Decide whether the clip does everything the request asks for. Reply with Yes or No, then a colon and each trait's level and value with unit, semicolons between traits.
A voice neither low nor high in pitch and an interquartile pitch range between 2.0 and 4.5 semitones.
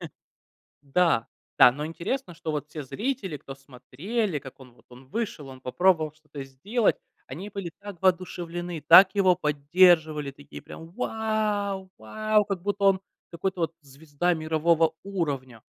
No: medium, 170 Hz; average, 5.2 semitones